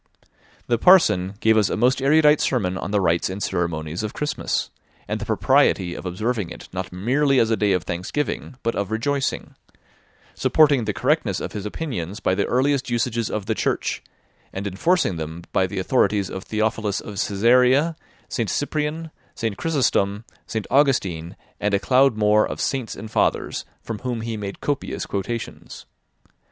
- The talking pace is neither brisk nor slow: Yes, average, 165 wpm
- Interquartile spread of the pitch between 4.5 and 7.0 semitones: Yes, average, 5.3 semitones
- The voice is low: Yes, low, 110 Hz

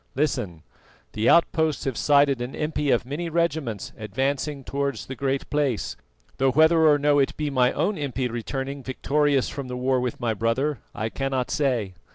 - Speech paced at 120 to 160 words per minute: No, average, 175 wpm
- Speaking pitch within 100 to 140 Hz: Yes, low, 135 Hz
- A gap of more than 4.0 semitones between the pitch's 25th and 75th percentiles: No, average, 2.9 semitones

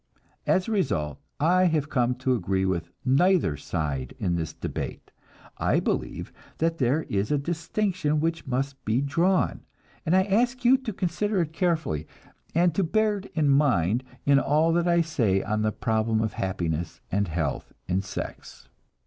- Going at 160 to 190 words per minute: Yes, average, 165 wpm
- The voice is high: No, medium, 140 Hz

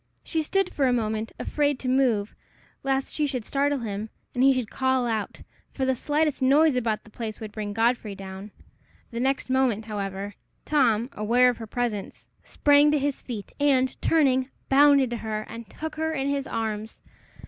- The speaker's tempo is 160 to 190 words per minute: Yes, average, 180 wpm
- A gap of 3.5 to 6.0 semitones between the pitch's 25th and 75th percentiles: Yes, average, 4.3 semitones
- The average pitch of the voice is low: No, very high, 250 Hz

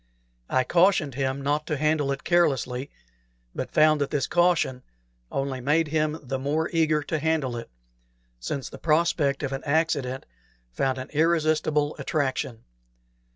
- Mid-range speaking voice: Yes, medium, 145 Hz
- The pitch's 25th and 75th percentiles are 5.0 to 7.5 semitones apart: No, average, 2.7 semitones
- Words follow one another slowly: No, average, 145 wpm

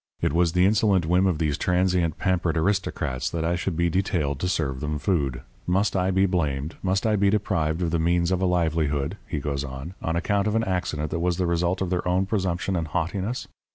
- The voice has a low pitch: Yes, very low, 90 Hz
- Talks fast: Yes, fast, 225 wpm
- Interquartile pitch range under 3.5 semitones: Yes, average, 2.9 semitones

